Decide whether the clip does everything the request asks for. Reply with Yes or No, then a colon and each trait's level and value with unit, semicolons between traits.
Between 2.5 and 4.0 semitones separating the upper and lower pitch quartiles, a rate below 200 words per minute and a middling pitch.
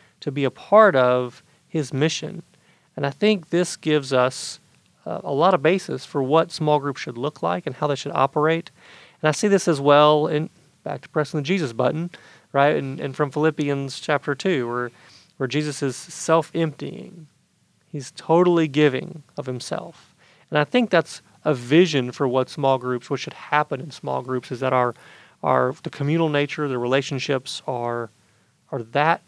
Yes: average, 3.2 semitones; average, 180 wpm; medium, 150 Hz